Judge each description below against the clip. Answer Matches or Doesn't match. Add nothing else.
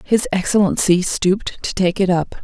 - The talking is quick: Doesn't match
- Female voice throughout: Matches